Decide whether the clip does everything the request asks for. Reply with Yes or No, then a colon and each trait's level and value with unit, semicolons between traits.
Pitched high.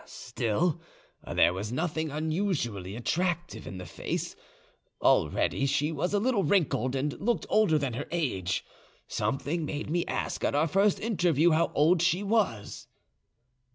No: medium, 160 Hz